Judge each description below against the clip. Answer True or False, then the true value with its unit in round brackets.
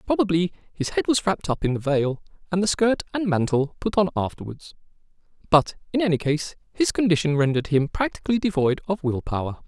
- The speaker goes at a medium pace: True (185 wpm)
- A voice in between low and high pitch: True (165 Hz)